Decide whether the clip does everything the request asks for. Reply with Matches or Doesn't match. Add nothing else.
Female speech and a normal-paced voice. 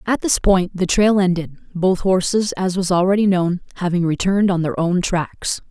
Matches